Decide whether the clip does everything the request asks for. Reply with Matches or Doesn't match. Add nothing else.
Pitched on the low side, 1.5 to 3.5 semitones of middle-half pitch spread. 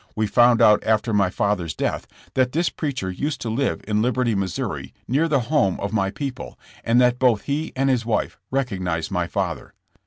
Doesn't match